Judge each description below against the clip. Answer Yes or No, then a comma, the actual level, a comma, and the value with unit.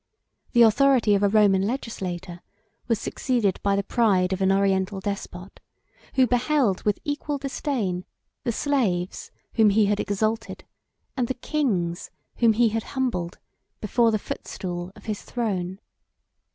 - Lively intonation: No, average, 4.2 semitones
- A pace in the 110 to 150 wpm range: Yes, average, 140 wpm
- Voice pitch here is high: Yes, high, 210 Hz